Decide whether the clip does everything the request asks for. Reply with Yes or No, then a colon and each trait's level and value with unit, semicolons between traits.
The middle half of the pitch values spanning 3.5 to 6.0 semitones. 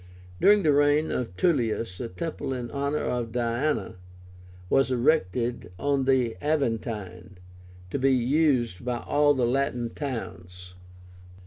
Yes: average, 3.9 semitones